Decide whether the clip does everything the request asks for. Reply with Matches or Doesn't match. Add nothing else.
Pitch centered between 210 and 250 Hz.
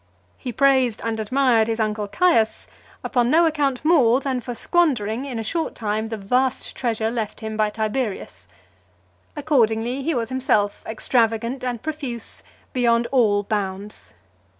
Matches